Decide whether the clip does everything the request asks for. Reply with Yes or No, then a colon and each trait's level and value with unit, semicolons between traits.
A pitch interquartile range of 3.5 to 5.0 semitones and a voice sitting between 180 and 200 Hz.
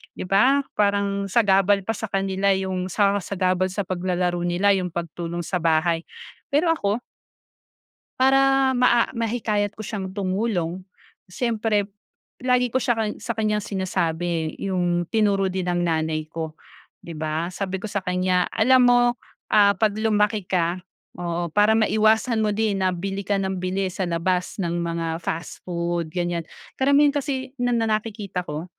Yes: average, 3.8 semitones; high, 195 Hz